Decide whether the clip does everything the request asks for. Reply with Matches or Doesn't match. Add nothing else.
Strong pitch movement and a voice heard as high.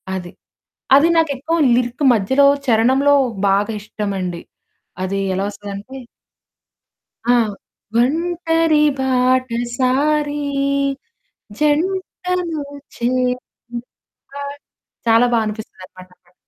Matches